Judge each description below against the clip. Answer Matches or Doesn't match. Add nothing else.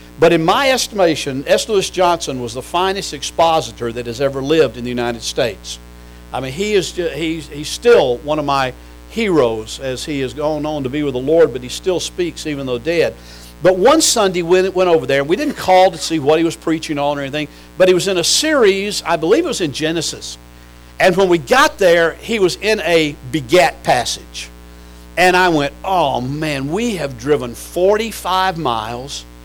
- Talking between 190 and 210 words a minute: Matches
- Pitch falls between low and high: Matches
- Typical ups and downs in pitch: Doesn't match